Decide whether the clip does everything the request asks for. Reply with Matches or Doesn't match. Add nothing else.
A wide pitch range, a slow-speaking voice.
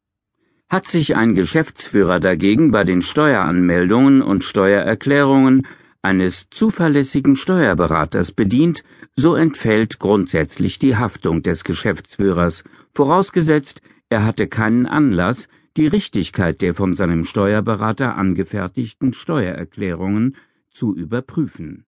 Matches